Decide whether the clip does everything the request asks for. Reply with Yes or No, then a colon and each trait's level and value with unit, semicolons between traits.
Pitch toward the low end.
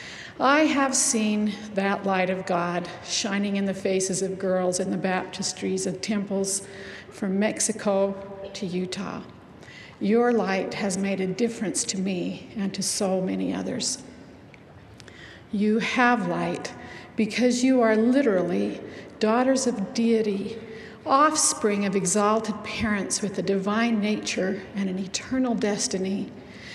No: high, 205 Hz